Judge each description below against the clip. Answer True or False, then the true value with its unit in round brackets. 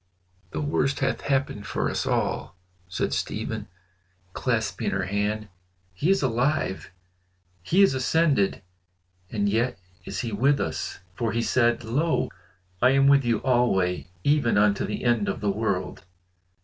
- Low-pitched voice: True (120 Hz)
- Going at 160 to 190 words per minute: False (145 wpm)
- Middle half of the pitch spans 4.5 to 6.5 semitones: True (5.1 semitones)